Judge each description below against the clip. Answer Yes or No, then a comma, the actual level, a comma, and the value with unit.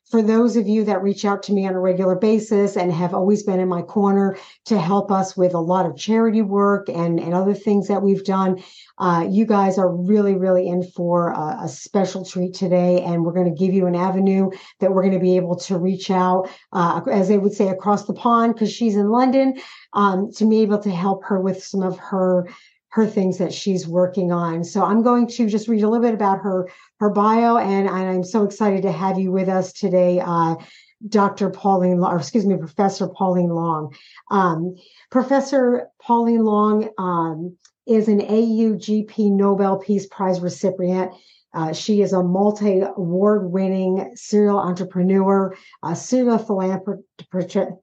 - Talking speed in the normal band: Yes, average, 190 wpm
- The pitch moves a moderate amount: No, narrow, 2.3 semitones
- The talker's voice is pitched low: No, high, 195 Hz